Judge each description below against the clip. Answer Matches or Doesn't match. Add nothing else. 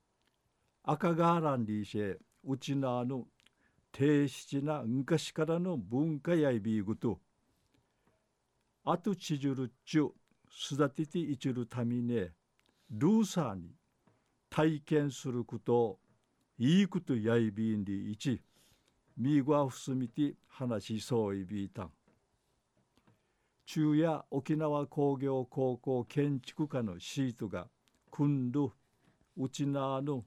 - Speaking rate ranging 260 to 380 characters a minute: Doesn't match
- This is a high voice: Doesn't match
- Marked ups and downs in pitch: Doesn't match